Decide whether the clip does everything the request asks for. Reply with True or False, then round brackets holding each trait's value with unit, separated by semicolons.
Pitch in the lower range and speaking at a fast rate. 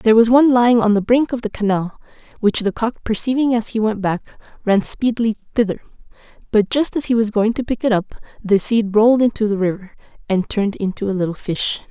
False (220 Hz; 215 wpm)